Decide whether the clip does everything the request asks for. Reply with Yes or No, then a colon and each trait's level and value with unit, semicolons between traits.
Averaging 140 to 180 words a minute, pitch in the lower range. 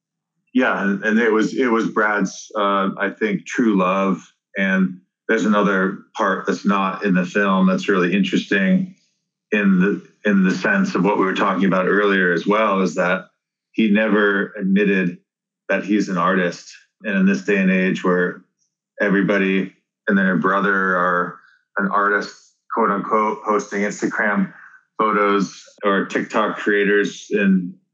Yes: average, 150 wpm; low, 100 Hz